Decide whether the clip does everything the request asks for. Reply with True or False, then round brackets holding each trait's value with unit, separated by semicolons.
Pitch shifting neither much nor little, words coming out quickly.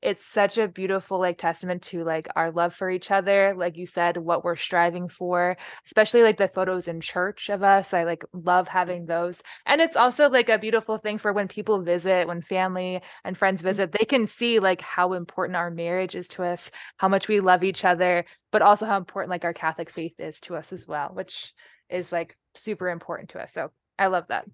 False (2.3 semitones; 220 wpm)